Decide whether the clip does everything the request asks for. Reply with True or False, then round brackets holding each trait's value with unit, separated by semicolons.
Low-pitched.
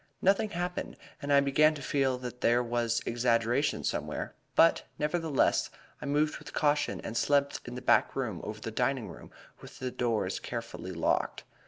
True (125 Hz)